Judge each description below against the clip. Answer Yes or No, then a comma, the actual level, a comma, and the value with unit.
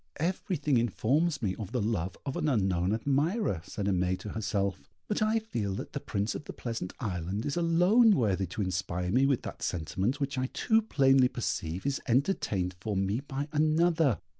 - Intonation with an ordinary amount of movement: No, wide, 7.6 semitones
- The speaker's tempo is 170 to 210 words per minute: Yes, average, 185 wpm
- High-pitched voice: No, low, 120 Hz